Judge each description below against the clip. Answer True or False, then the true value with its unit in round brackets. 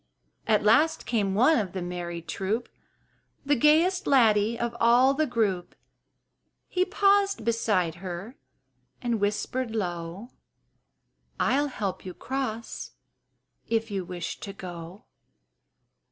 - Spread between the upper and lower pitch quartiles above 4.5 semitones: True (5.5 semitones)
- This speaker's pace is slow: True (115 wpm)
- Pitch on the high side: True (225 Hz)